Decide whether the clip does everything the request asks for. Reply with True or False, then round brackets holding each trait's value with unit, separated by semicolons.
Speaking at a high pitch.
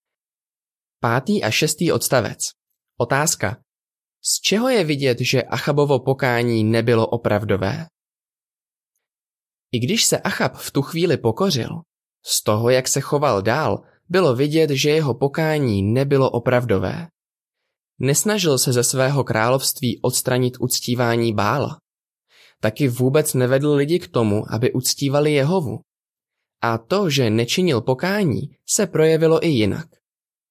False (135 Hz)